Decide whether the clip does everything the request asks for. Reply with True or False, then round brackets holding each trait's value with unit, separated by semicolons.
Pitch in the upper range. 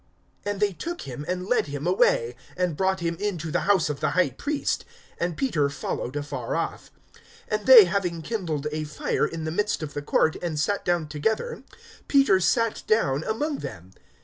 False (170 Hz)